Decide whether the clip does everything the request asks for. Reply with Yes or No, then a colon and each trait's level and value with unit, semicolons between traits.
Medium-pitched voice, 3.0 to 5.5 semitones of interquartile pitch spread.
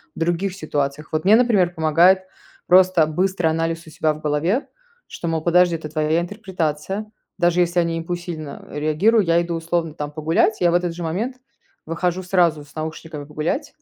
No: medium, 170 Hz; narrow, 2.5 semitones